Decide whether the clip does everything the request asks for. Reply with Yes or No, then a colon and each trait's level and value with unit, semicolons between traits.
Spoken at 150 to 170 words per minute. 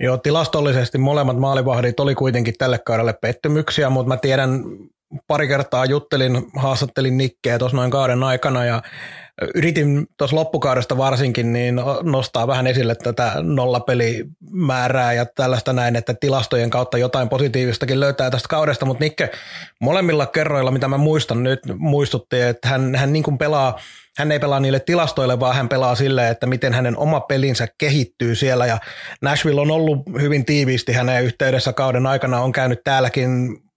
Yes: fast, 155 wpm